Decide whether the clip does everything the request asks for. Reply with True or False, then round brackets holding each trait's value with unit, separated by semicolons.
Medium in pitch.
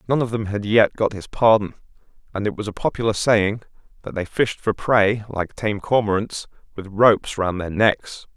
False (105 Hz)